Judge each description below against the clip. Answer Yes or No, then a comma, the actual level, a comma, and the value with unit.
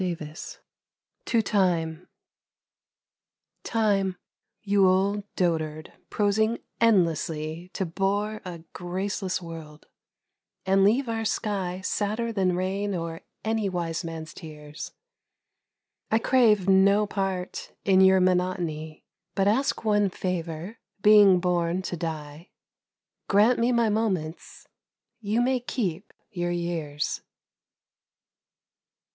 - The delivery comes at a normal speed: No, slow, 105 wpm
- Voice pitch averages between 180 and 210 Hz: Yes, high, 190 Hz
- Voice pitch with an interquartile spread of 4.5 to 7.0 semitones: No, average, 3.7 semitones